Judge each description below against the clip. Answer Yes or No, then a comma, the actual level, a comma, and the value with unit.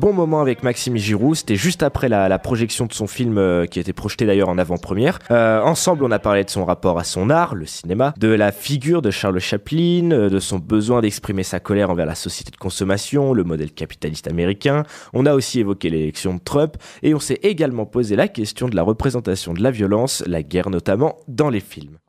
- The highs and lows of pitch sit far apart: Yes, wide, 6.0 semitones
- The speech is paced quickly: Yes, fast, 225 wpm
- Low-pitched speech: Yes, low, 105 Hz